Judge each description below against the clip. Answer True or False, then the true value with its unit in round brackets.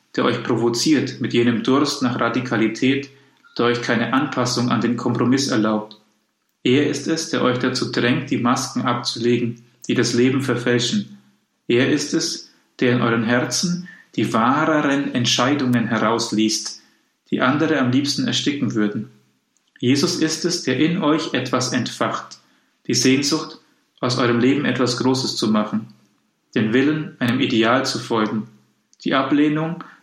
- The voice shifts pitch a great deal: False (2.7 semitones)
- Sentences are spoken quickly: False (145 wpm)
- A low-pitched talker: True (125 Hz)